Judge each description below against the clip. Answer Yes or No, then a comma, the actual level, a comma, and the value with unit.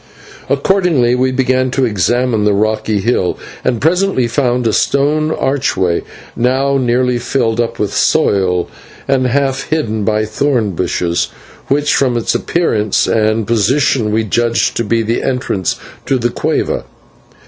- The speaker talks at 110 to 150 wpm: Yes, average, 140 wpm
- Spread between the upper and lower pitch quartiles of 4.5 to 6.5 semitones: No, average, 3.8 semitones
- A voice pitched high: No, low, 120 Hz